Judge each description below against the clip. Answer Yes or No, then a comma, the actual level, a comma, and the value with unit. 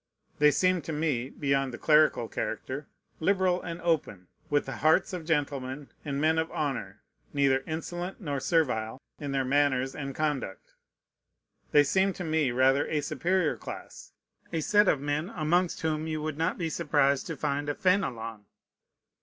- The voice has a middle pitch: Yes, medium, 150 Hz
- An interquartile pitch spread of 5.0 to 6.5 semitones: No, average, 3.1 semitones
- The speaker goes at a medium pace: Yes, average, 160 wpm